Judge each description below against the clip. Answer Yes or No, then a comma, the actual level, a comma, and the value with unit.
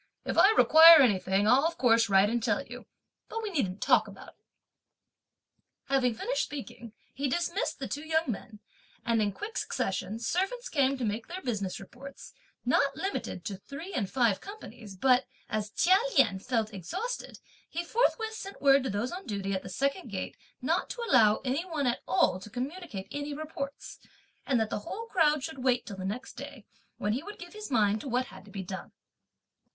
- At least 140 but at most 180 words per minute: No, average, 195 wpm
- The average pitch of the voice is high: Yes, very high, 255 Hz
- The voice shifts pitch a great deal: Yes, wide, 7.6 semitones